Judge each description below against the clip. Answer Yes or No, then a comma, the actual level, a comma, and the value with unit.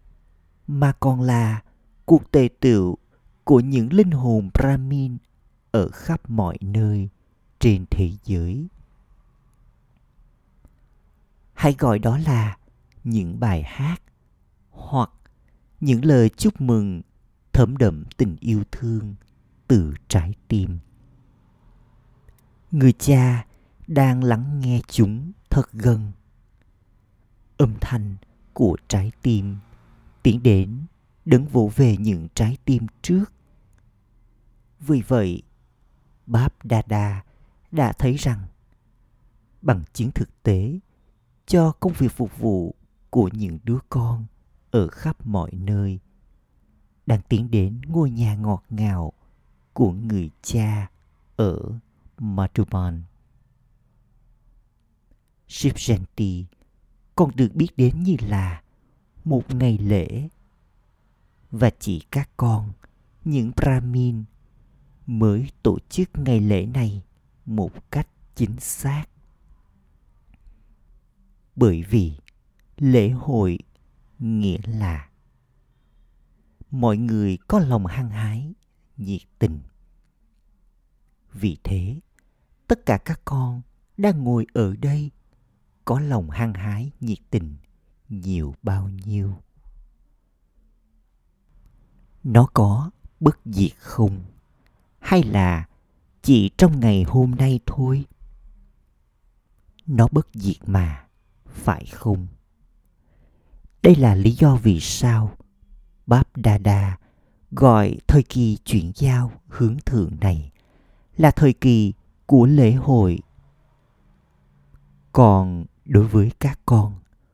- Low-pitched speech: Yes, low, 110 Hz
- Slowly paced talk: Yes, slow, 100 wpm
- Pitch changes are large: No, average, 4.9 semitones